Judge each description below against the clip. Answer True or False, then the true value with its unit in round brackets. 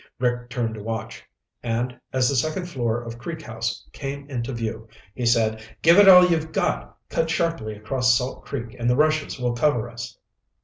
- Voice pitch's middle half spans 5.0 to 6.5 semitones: False (4.4 semitones)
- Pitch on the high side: False (125 Hz)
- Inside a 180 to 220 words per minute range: True (185 wpm)